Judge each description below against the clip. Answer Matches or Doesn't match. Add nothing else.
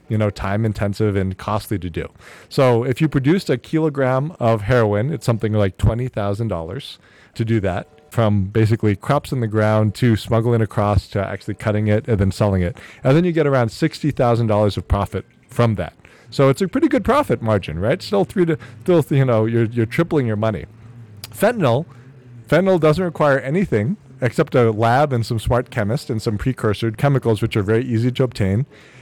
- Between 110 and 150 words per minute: Doesn't match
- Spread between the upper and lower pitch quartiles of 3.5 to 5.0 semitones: Matches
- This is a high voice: Doesn't match